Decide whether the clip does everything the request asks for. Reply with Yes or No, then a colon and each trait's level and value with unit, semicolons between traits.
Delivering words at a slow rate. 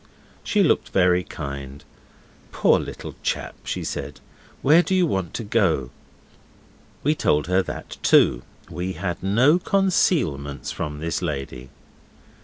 Yes: slow, 130 wpm